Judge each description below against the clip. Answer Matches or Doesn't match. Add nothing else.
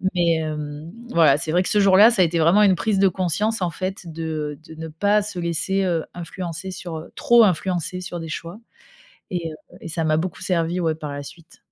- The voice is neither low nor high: Matches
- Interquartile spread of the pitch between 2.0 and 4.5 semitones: Matches